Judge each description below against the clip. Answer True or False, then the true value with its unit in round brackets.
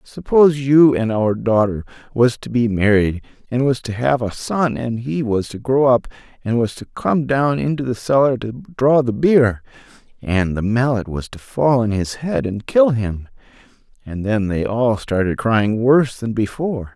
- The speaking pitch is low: True (120 Hz)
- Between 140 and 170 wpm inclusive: False (190 wpm)